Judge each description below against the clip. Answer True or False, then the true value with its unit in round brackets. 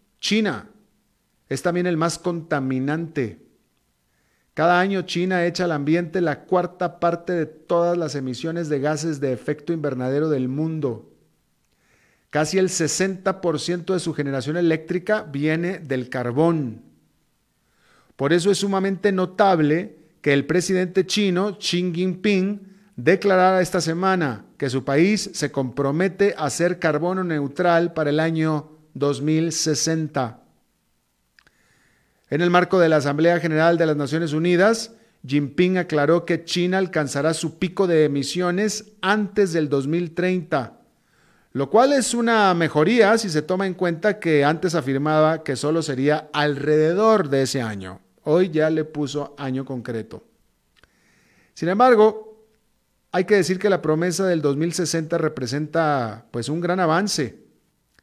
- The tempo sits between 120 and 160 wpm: True (130 wpm)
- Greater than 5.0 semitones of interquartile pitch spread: False (3.8 semitones)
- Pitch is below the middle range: False (165 Hz)